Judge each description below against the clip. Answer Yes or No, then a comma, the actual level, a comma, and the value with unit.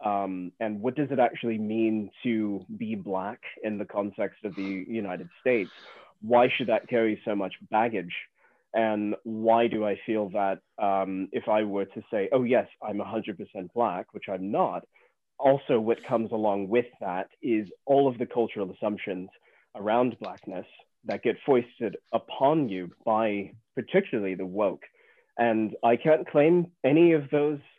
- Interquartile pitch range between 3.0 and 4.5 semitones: Yes, average, 3.3 semitones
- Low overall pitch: Yes, low, 110 Hz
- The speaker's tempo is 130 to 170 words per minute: Yes, average, 160 wpm